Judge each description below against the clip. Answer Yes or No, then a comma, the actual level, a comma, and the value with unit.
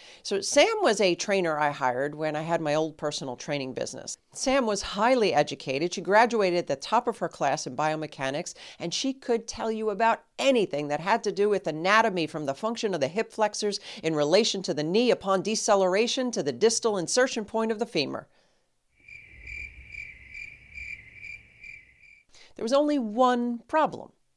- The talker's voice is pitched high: Yes, high, 200 Hz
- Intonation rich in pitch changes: Yes, wide, 6.6 semitones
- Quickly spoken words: No, average, 170 wpm